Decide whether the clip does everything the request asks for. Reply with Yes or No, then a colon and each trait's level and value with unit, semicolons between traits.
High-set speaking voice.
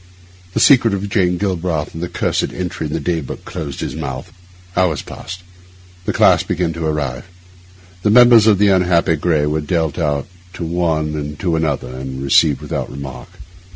No: very low, 80 Hz